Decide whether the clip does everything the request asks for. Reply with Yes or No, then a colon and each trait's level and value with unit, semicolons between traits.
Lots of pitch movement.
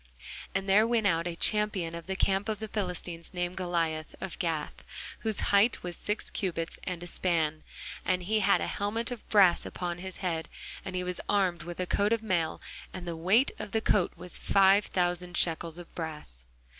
No: average, 3.0 semitones